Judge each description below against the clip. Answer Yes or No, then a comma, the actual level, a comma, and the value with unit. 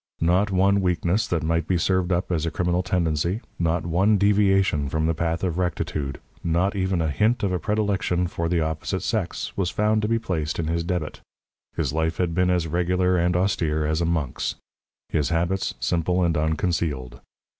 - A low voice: Yes, very low, 85 Hz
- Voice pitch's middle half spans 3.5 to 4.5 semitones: No, narrow, 2.4 semitones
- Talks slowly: No, average, 190 wpm